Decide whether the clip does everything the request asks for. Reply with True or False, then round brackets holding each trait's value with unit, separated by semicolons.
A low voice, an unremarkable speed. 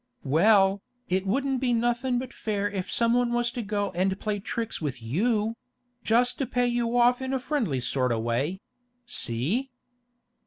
False (225 Hz; 155 wpm)